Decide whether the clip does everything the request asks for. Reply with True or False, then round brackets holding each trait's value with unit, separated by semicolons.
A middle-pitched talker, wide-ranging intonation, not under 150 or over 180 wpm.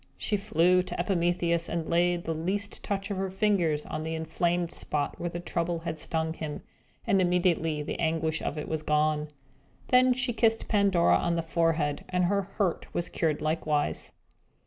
False (170 Hz; 2.7 semitones; 175 wpm)